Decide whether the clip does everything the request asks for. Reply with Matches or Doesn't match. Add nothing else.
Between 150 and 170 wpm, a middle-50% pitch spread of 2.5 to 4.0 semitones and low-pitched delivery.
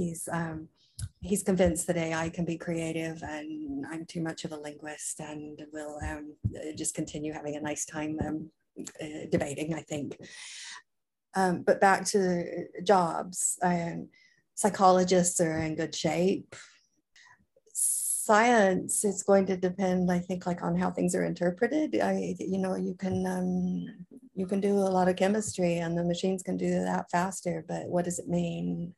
Doesn't match